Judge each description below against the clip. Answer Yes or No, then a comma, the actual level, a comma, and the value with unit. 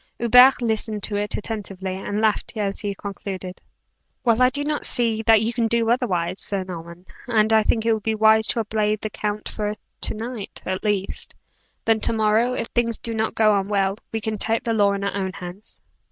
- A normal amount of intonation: No, narrow, 2.2 semitones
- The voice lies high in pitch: Yes, high, 215 Hz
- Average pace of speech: No, fast, 210 wpm